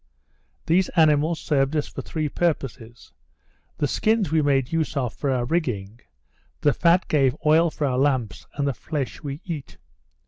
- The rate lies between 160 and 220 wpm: Yes, average, 165 wpm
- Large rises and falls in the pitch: No, average, 3.5 semitones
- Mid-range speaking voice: Yes, medium, 145 Hz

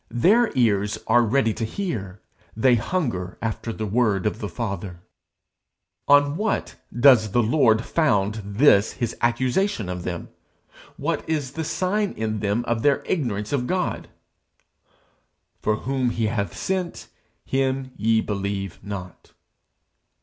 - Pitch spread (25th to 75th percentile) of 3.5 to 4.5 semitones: No, average, 5.0 semitones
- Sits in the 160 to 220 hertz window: No, low, 115 Hz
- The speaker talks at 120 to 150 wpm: Yes, slow, 135 wpm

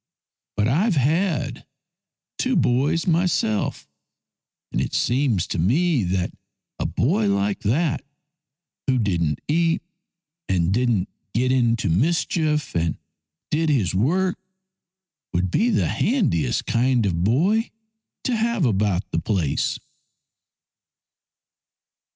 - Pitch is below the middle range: Yes, low, 125 Hz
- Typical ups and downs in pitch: No, wide, 8.7 semitones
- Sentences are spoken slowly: Yes, slow, 110 wpm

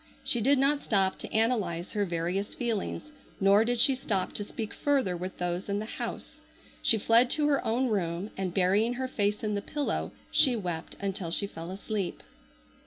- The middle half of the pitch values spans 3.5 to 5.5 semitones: Yes, average, 4.3 semitones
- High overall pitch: Yes, high, 205 Hz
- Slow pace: No, average, 185 wpm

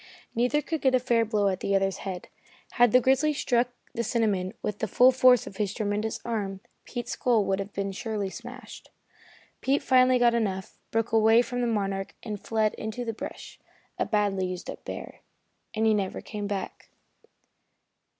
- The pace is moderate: Yes, average, 180 wpm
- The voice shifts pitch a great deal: No, average, 3.4 semitones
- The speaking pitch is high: Yes, high, 220 Hz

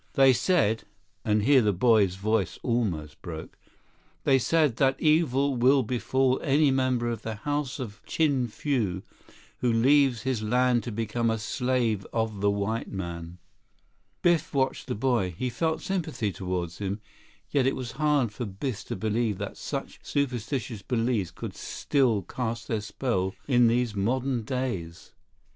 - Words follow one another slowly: No, average, 150 wpm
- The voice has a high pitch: No, low, 120 Hz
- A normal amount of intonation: Yes, average, 4.2 semitones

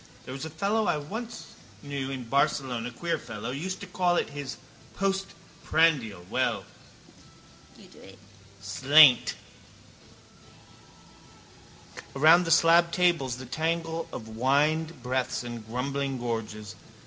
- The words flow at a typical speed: No, slow, 110 wpm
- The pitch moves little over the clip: No, average, 5.2 semitones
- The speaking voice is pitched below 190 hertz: Yes, medium, 140 Hz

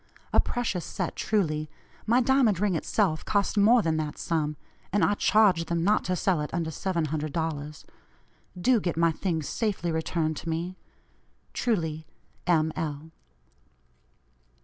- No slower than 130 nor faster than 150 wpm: Yes, average, 140 wpm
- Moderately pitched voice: Yes, medium, 170 Hz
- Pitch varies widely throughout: No, average, 4.4 semitones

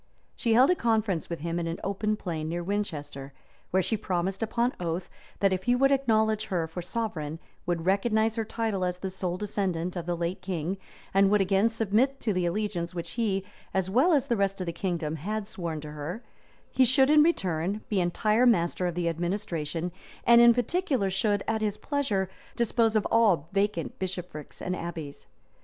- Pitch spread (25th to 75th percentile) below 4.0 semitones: No, average, 4.3 semitones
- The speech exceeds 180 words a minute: Yes, average, 190 wpm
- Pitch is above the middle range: Yes, high, 195 Hz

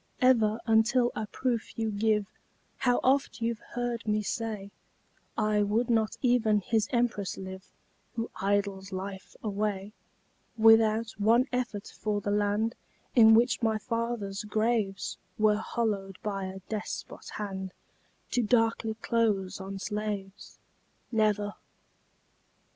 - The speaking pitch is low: No, high, 215 Hz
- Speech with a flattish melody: Yes, narrow, 2.1 semitones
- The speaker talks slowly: Yes, slow, 120 wpm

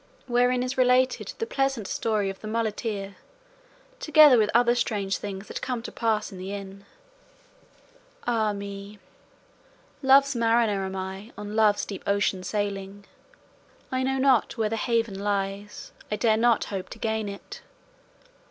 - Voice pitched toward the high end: Yes, high, 215 Hz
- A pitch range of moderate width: Yes, average, 3.3 semitones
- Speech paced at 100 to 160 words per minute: Yes, average, 150 wpm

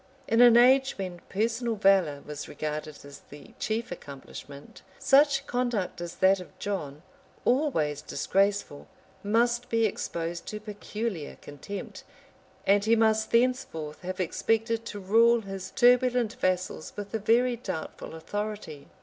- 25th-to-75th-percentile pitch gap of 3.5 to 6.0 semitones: Yes, wide, 5.4 semitones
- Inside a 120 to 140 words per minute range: Yes, slow, 135 wpm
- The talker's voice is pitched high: Yes, high, 205 Hz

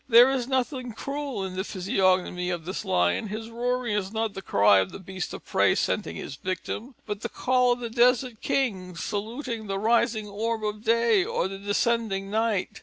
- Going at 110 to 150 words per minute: No, average, 190 wpm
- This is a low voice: No, high, 215 Hz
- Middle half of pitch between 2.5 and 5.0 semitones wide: Yes, average, 3.9 semitones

